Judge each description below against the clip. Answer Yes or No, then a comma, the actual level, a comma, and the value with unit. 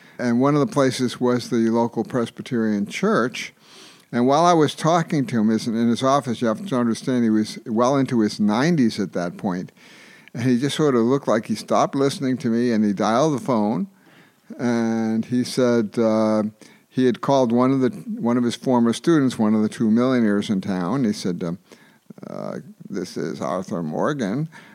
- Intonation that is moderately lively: Yes, average, 3.3 semitones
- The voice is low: Yes, low, 120 Hz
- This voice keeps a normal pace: Yes, average, 195 wpm